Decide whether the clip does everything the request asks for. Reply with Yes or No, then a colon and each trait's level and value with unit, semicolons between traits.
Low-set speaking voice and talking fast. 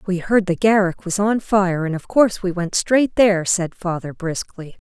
No: high, 190 Hz; fast, 210 wpm